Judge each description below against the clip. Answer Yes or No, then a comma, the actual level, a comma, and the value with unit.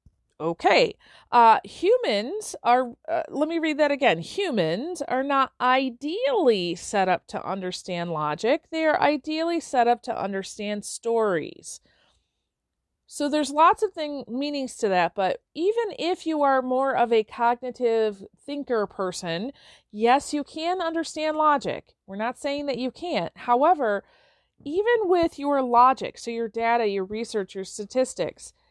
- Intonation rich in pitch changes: Yes, wide, 6.0 semitones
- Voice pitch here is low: No, very high, 255 Hz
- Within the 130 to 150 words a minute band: Yes, average, 145 wpm